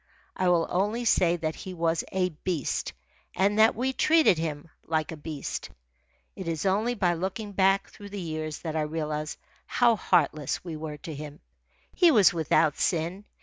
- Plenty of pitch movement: No, average, 4.1 semitones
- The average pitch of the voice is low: No, medium, 170 Hz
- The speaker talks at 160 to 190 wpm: Yes, average, 175 wpm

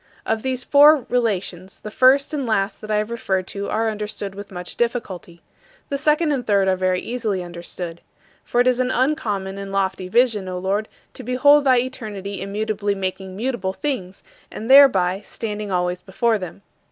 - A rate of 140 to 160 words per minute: No, average, 175 wpm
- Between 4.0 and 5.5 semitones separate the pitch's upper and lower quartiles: Yes, average, 4.6 semitones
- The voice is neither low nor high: No, high, 210 Hz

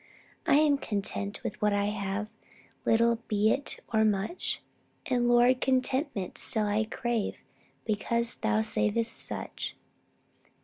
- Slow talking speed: Yes, slow, 125 wpm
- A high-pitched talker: Yes, high, 220 Hz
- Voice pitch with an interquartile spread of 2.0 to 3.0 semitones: Yes, narrow, 2.6 semitones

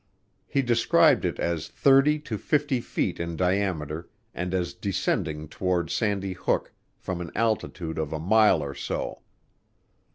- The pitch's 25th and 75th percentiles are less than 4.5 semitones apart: No, average, 5.1 semitones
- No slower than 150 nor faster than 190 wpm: No, average, 140 wpm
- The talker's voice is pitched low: Yes, very low, 90 Hz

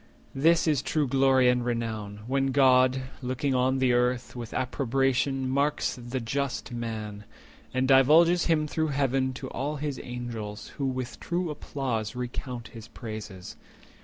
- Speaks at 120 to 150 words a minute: Yes, average, 145 wpm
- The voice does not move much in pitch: Yes, narrow, 2.3 semitones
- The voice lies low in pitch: Yes, low, 130 Hz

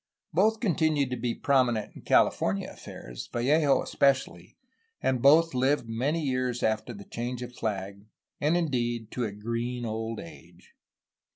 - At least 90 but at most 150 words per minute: Yes, average, 145 wpm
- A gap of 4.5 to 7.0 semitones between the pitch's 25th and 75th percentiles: No, average, 4.1 semitones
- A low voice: Yes, low, 125 Hz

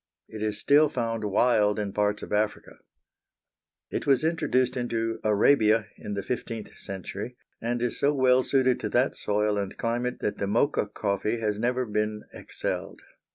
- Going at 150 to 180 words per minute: Yes, average, 160 wpm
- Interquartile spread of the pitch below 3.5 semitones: Yes, average, 3.1 semitones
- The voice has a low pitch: Yes, low, 115 Hz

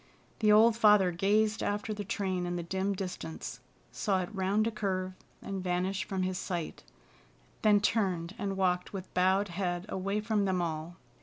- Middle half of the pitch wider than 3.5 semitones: No, narrow, 2.4 semitones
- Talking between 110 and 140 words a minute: No, average, 170 wpm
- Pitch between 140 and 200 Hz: Yes, high, 190 Hz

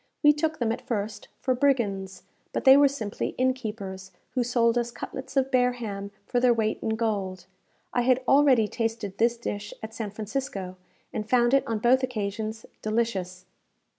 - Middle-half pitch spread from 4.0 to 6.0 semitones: No, average, 3.6 semitones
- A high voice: Yes, high, 230 Hz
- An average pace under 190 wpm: Yes, average, 175 wpm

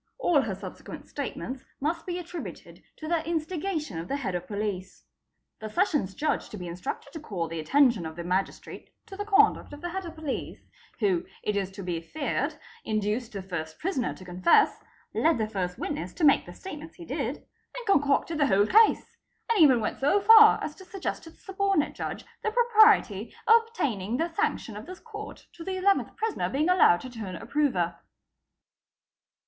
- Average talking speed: Yes, average, 190 wpm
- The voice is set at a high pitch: Yes, very high, 285 Hz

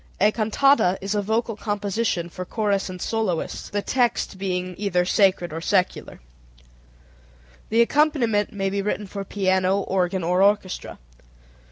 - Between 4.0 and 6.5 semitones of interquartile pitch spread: No, narrow, 2.5 semitones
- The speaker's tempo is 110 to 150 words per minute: Yes, average, 140 wpm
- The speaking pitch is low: No, high, 200 Hz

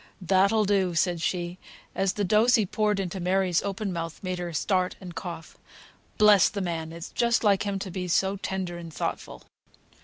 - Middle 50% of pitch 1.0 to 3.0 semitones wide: Yes, narrow, 2.5 semitones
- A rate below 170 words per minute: No, average, 185 wpm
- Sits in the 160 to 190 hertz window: Yes, medium, 185 Hz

